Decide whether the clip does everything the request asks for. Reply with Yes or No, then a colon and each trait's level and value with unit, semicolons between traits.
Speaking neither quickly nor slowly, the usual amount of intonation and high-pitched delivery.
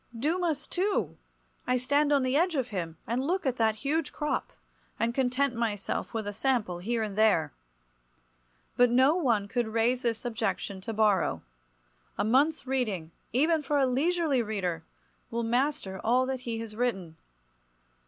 Yes: average, 155 wpm; average, 4.2 semitones; high, 245 Hz